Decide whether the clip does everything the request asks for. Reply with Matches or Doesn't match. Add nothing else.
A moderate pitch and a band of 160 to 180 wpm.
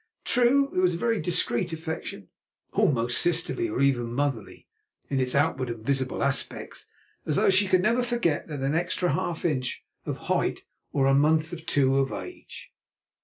Matches